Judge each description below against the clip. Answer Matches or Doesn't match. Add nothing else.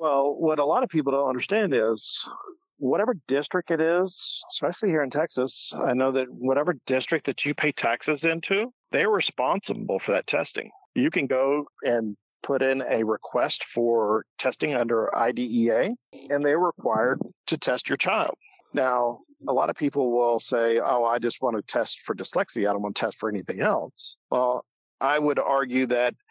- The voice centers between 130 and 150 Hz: Matches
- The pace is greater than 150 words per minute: Matches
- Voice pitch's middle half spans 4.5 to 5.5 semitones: Matches